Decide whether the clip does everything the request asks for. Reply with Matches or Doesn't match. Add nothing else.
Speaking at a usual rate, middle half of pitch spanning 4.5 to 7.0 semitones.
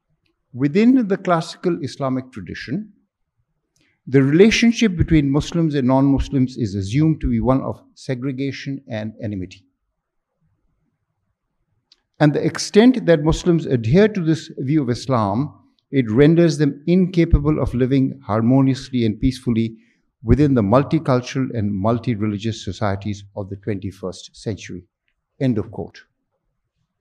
Doesn't match